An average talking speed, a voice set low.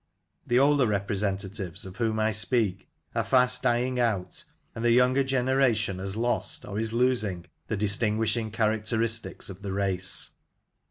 Yes: average, 150 wpm; low, 110 Hz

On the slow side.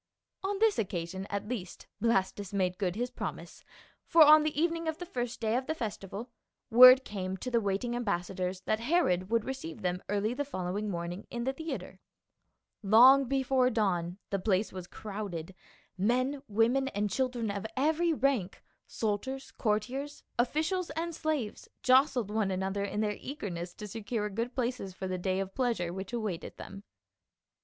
No: average, 170 wpm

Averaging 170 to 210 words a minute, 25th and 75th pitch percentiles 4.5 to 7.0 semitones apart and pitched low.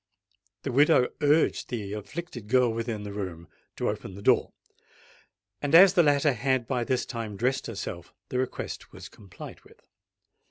No: average, 160 wpm; average, 5.2 semitones; low, 120 Hz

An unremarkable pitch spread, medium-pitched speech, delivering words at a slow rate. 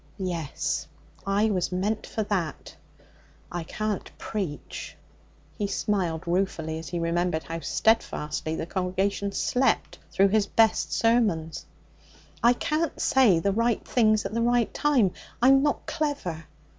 No: average, 5.0 semitones; high, 200 Hz; slow, 130 wpm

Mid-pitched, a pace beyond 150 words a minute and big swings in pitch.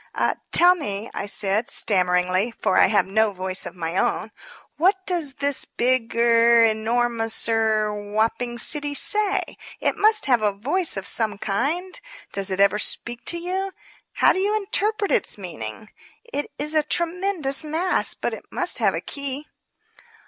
No: high, 240 Hz; average, 160 wpm; wide, 8.4 semitones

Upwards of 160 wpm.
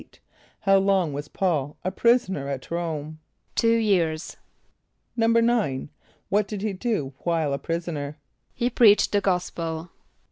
No: slow, 135 wpm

